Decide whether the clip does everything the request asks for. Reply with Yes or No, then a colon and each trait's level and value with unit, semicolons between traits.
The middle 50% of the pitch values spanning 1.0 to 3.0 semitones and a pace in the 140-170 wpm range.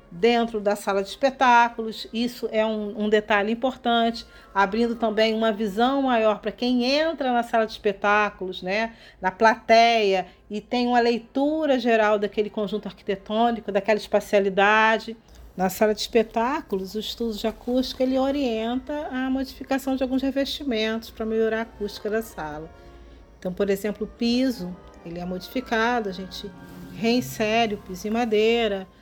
Yes: narrow, 2.5 semitones; average, 150 wpm